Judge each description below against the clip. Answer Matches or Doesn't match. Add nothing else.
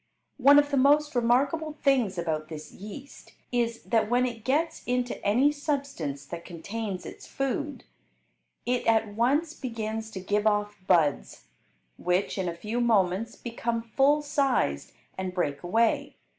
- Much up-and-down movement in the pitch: Matches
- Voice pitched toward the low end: Doesn't match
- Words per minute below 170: Matches